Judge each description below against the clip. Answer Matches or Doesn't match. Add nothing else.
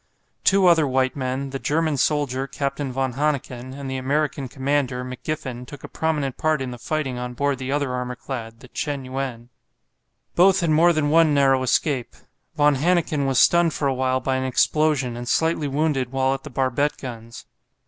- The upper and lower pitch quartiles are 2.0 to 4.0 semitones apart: Matches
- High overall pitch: Doesn't match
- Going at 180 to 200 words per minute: Matches